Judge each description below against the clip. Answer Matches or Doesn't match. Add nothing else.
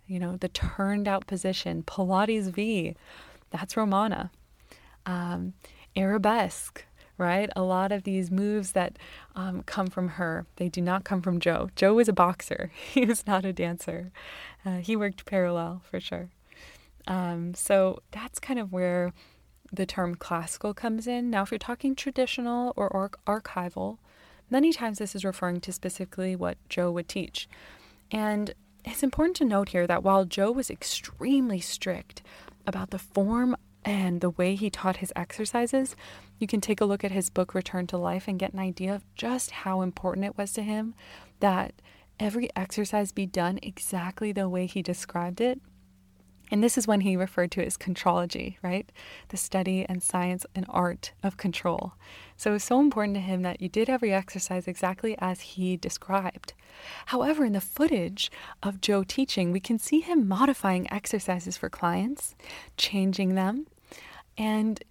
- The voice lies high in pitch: Matches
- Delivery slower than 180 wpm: Matches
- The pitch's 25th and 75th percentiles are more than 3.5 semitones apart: Doesn't match